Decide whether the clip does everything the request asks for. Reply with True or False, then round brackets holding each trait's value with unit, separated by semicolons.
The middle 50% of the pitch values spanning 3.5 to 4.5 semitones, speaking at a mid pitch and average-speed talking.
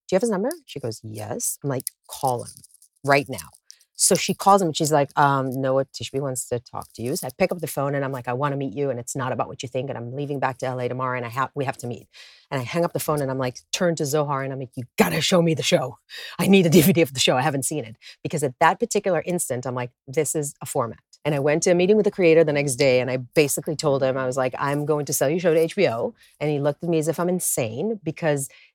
False (3.9 semitones; 145 Hz; 305 wpm)